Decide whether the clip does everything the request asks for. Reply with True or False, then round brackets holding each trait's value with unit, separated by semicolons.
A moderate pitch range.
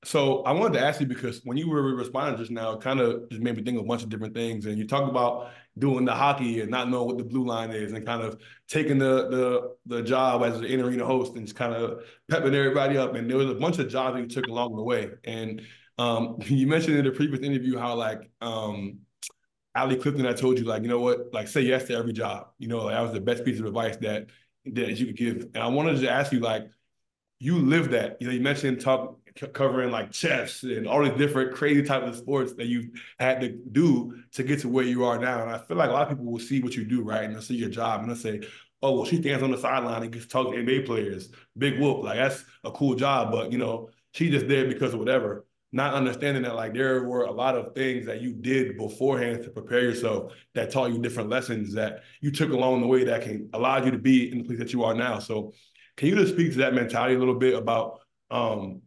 False (2.3 semitones)